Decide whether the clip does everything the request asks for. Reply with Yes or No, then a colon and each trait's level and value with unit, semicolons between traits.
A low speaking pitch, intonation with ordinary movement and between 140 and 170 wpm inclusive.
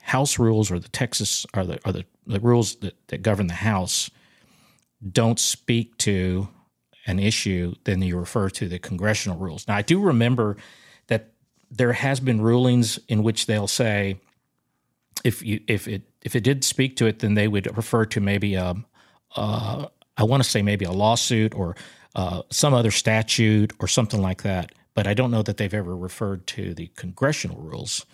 No: low, 110 Hz; average, 3.5 semitones; average, 185 wpm